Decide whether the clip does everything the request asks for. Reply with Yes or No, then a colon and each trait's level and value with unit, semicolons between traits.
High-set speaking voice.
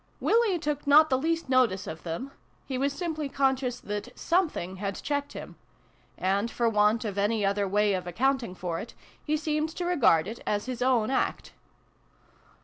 Yes: very high, 250 Hz